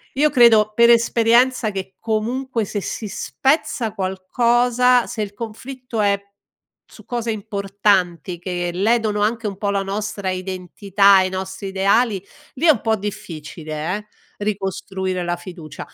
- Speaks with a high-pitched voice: Yes, high, 205 Hz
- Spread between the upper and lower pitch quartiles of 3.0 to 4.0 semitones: Yes, average, 3.5 semitones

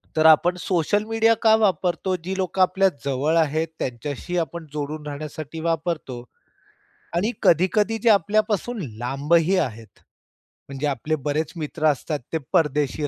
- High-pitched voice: No, medium, 160 Hz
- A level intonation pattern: No, average, 4.1 semitones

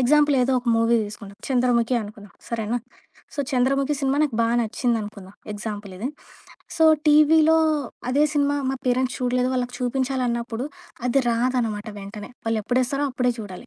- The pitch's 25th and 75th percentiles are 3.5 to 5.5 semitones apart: No, average, 3.1 semitones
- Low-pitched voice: No, high, 245 Hz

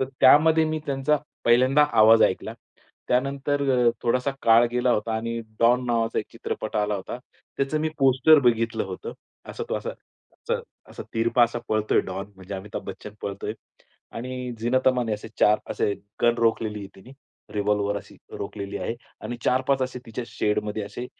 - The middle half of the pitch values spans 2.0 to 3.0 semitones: No, average, 3.4 semitones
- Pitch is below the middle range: Yes, low, 115 Hz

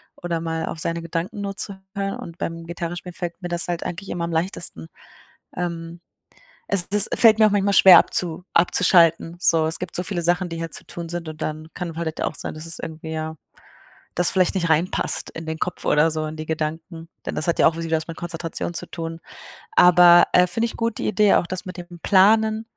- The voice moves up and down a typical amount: No, narrow, 1.9 semitones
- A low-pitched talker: No, medium, 170 Hz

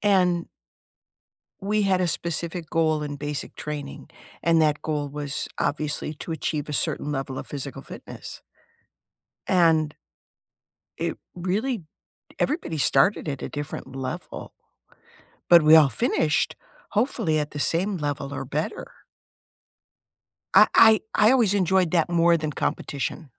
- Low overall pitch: No, medium, 155 Hz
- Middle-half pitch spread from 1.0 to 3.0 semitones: No, average, 3.5 semitones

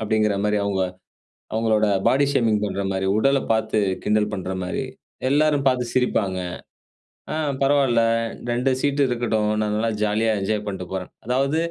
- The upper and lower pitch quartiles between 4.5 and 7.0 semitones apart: No, average, 3.6 semitones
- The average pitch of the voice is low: Yes, low, 110 Hz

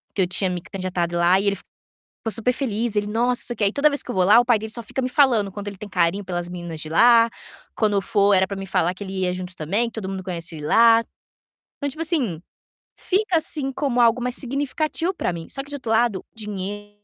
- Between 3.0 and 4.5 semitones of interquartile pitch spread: No, average, 4.9 semitones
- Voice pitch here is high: Yes, high, 210 Hz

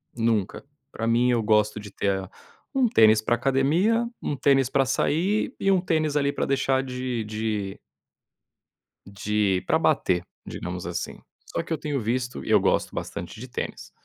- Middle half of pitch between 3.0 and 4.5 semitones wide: No, average, 4.9 semitones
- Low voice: Yes, low, 125 Hz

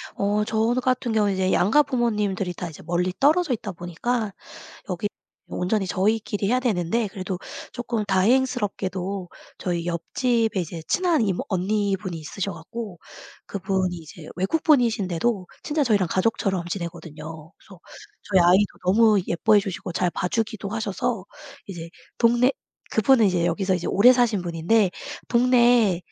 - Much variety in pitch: No, average, 4.3 semitones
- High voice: Yes, high, 200 Hz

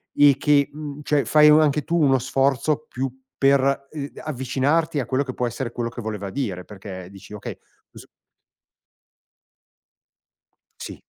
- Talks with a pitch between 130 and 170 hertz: Yes, low, 135 Hz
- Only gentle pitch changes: No, average, 3.7 semitones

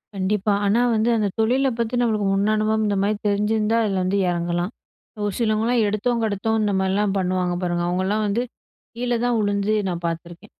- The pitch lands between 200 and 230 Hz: Yes, high, 205 Hz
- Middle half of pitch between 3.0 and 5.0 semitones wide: No, narrow, 2.6 semitones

